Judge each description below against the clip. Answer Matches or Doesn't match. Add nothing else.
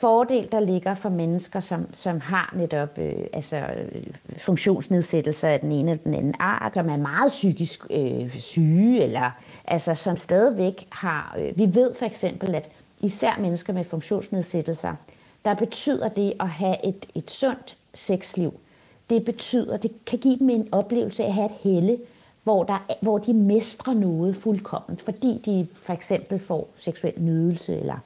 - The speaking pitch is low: Doesn't match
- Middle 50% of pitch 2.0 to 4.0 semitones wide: Doesn't match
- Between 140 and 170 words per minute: Matches